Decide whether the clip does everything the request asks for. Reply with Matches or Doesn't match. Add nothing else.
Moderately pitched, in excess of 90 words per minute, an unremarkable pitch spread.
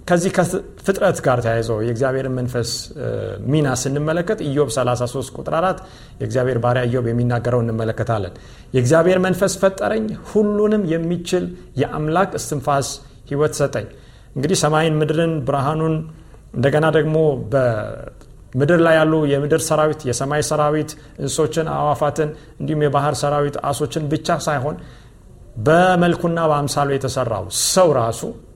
Matches